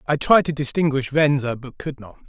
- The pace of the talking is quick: Yes, fast, 210 wpm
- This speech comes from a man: Yes, male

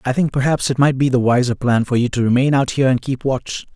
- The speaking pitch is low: Yes, low, 130 Hz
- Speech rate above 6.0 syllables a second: Yes, 6.2 syllables/s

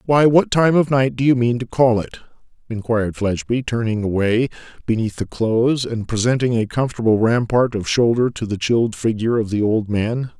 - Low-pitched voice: Yes, low, 115 Hz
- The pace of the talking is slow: No, average, 190 wpm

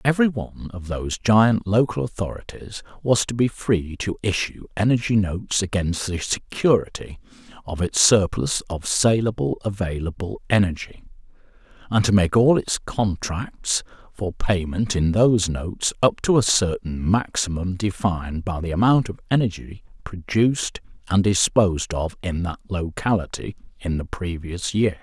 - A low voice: Yes, low, 100 Hz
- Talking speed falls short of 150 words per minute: Yes, average, 140 wpm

